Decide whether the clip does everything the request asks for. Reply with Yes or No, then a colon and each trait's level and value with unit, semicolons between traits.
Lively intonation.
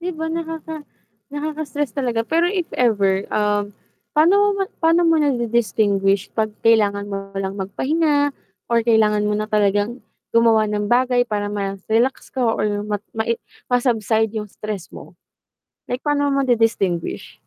Yes: wide, 5.7 semitones